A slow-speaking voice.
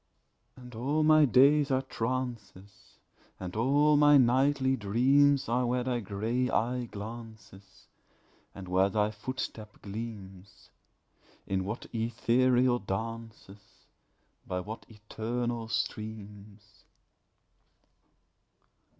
Yes: slow, 95 wpm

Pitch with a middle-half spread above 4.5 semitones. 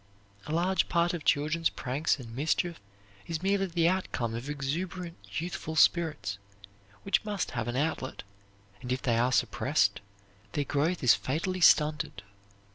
Yes: average, 4.9 semitones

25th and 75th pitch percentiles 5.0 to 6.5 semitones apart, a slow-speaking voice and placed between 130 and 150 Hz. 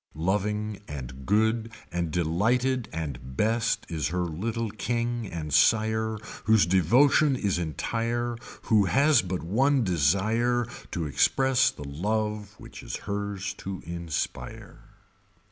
No: average, 5.3 semitones; slow, 120 wpm; low, 105 Hz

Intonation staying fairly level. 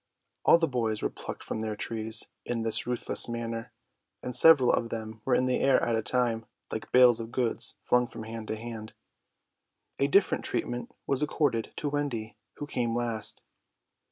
Yes: narrow, 2.2 semitones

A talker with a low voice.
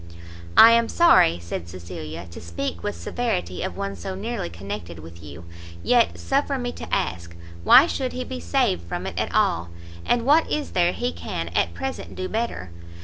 Yes: very low, 95 Hz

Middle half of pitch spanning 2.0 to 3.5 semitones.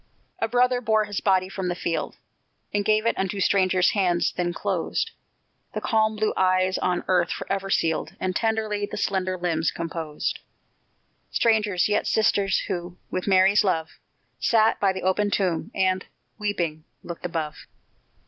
Yes: average, 2.8 semitones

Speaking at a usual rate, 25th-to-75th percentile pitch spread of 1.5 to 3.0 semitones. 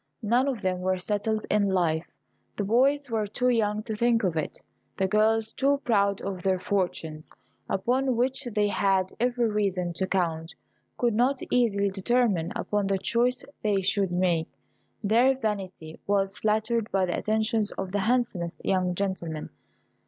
No: average, 160 wpm; average, 3.8 semitones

